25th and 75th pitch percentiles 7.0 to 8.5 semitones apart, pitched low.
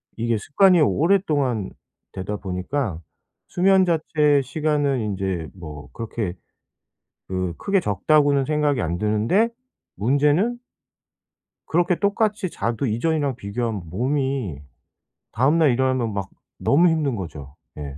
Yes: wide, 7.4 semitones; low, 130 Hz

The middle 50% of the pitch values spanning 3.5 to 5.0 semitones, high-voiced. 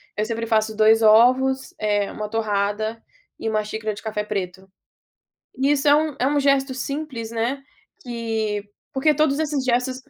Yes: average, 3.9 semitones; high, 230 Hz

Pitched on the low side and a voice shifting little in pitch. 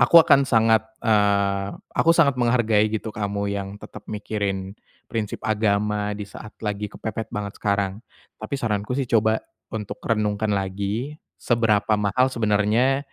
Yes: low, 105 Hz; narrow, 1.9 semitones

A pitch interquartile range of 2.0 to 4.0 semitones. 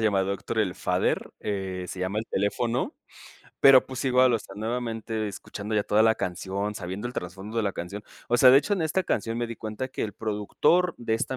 Yes: average, 3.6 semitones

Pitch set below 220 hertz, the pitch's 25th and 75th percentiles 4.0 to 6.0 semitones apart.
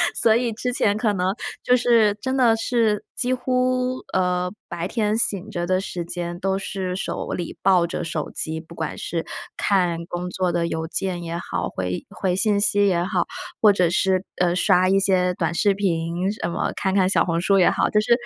No: high, 190 Hz; average, 3.4 semitones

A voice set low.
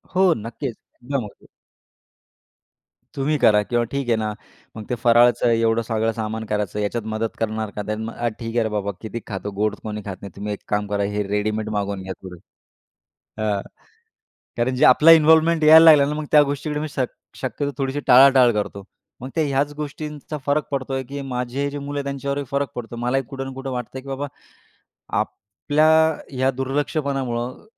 Yes: low, 125 Hz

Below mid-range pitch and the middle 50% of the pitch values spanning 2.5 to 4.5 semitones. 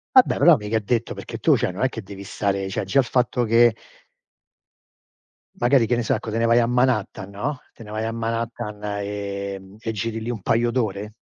Yes: low, 115 Hz; average, 2.9 semitones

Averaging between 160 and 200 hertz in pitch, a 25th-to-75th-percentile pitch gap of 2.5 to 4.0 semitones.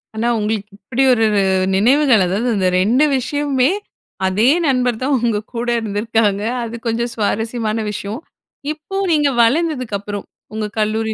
No: high, 230 Hz; average, 3.3 semitones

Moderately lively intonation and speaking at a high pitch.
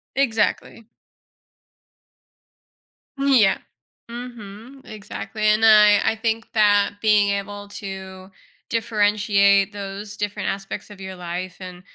No: narrow, 1.9 semitones; high, 205 Hz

